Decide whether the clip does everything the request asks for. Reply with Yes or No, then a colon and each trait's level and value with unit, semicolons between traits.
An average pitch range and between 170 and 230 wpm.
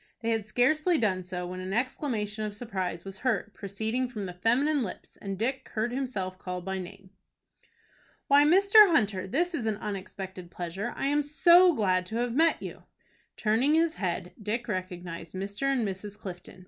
No: wide, 5.8 semitones; average, 175 wpm